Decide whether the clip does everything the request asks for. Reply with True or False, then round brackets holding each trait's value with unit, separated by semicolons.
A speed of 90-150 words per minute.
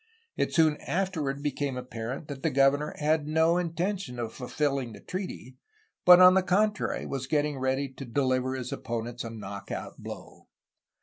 False (165 wpm)